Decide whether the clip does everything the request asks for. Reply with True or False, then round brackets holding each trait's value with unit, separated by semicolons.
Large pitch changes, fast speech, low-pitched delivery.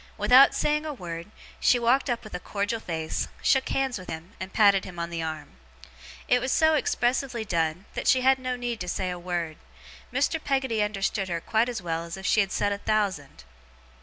False (6.1 semitones; 210 wpm; 205 Hz)